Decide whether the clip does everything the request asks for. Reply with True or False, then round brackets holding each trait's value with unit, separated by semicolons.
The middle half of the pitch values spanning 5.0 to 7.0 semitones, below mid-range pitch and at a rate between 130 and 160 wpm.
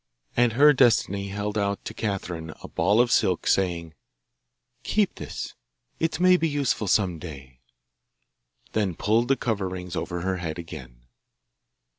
True (5.5 semitones; 100 Hz; 140 wpm)